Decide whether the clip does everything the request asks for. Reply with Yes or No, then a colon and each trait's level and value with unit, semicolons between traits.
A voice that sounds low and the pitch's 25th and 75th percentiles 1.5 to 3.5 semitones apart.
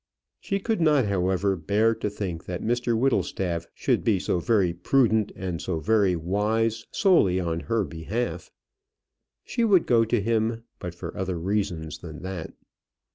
No: low, 100 Hz; average, 4.5 semitones